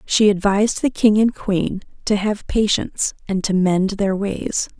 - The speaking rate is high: No, average, 175 wpm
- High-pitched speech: Yes, high, 200 Hz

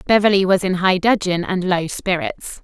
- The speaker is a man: No, female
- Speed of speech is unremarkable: Yes, average, 180 wpm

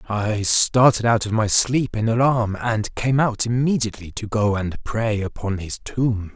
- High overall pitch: No, low, 110 Hz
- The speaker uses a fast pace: No, average, 180 wpm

